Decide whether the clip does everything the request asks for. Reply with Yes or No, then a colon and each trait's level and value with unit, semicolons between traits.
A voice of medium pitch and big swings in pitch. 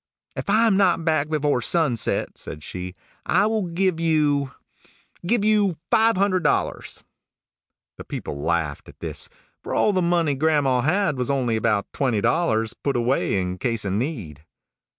Yes: medium, 145 Hz; wide, 7.7 semitones